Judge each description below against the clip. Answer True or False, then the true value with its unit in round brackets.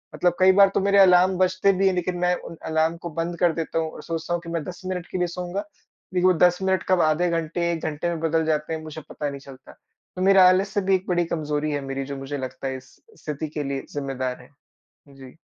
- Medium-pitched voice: True (170 Hz)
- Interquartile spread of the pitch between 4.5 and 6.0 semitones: False (3.3 semitones)